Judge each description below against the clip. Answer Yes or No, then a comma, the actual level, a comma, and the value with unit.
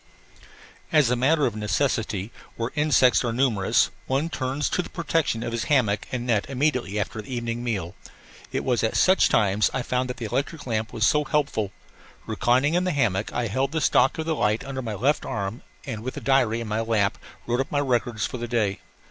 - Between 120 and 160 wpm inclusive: No, fast, 205 wpm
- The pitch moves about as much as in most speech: Yes, average, 3.9 semitones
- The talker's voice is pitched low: Yes, low, 120 Hz